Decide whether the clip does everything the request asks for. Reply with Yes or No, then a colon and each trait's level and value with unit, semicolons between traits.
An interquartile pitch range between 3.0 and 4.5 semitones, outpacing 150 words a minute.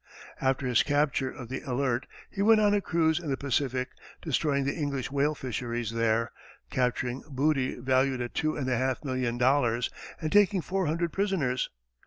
Yes: average, 3.6 semitones; average, 175 wpm